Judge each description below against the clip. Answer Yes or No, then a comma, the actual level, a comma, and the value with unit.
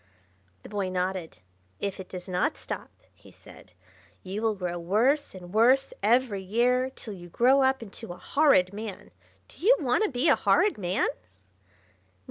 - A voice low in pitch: No, high, 215 Hz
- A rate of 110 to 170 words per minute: Yes, average, 165 wpm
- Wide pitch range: Yes, wide, 5.8 semitones